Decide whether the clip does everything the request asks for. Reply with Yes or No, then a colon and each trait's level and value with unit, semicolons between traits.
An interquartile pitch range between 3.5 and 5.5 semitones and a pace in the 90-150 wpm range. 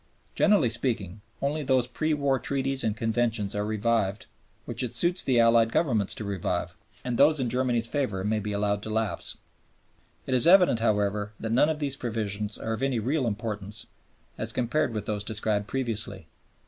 No: average, 4.0 semitones; average, 175 wpm